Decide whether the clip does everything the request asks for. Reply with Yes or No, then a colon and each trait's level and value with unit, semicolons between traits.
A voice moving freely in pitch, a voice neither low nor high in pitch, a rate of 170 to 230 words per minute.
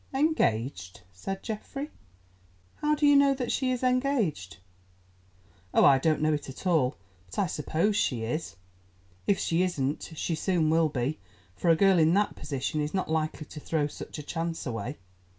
Yes: wide, 6.0 semitones; medium, 160 Hz; average, 175 wpm